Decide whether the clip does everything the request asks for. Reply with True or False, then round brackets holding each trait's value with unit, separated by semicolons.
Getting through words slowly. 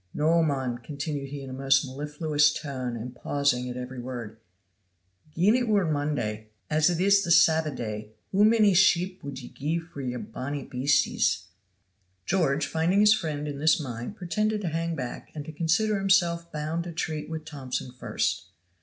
False (175 wpm)